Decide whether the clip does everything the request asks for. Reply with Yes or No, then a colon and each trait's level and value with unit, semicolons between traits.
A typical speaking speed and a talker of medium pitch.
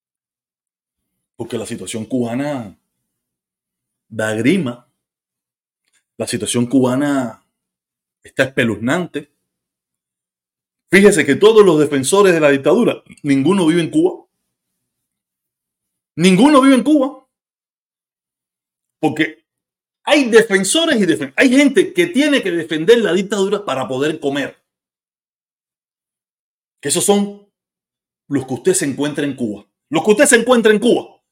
No: slow, 115 wpm; medium, 170 Hz